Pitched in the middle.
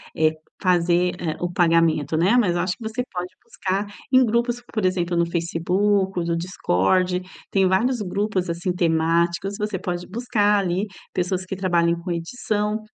Yes: medium, 180 Hz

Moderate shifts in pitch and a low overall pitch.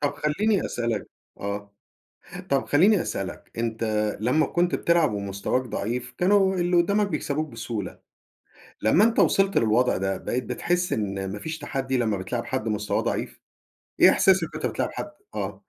No: wide, 8.4 semitones; low, 130 Hz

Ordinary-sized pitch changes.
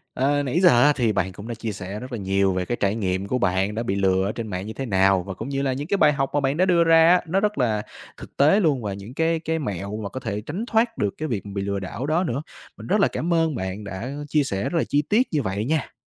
No: wide, 7.7 semitones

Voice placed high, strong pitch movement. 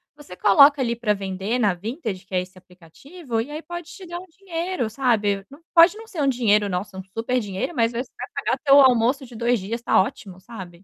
Yes: high, 235 Hz; wide, 6.4 semitones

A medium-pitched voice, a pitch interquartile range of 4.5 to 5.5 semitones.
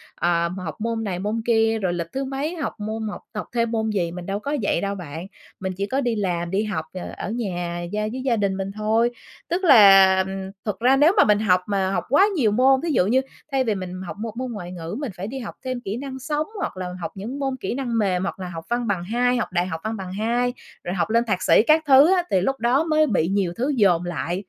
No: high, 215 Hz; average, 4.9 semitones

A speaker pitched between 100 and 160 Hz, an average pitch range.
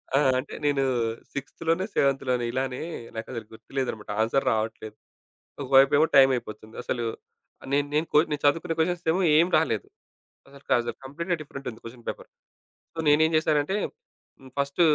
Yes: low, 135 Hz; average, 4.1 semitones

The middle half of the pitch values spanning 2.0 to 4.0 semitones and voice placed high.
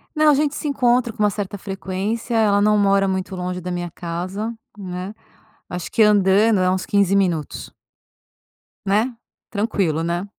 Yes: average, 3.0 semitones; high, 200 Hz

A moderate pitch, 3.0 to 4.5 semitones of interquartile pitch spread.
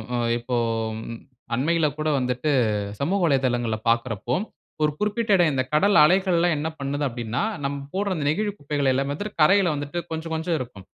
No: medium, 150 Hz; average, 5.3 semitones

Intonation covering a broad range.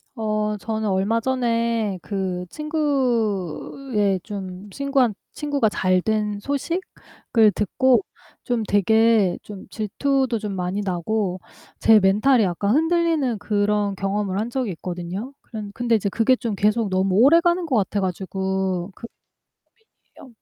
No: average, 4.1 semitones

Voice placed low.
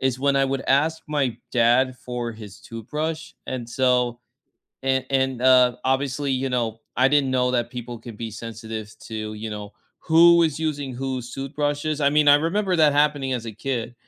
Yes: low, 130 Hz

